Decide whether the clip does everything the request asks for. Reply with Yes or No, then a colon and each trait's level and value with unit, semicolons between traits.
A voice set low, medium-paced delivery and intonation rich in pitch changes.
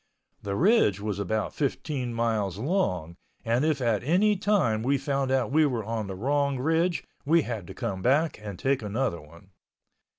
Yes: low, 125 Hz; average, 175 wpm; wide, 6.0 semitones